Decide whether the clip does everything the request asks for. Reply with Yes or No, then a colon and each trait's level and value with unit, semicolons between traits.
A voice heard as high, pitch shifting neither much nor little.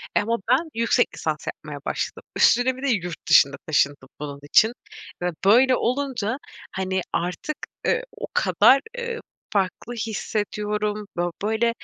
Yes: high, 215 Hz; average, 4.9 semitones